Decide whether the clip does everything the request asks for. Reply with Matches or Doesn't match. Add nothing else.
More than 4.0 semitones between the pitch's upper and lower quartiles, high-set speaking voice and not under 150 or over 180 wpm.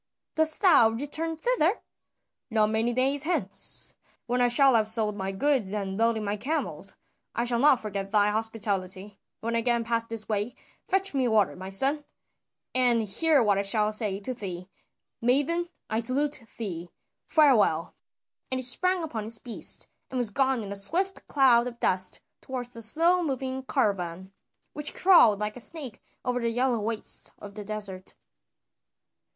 Matches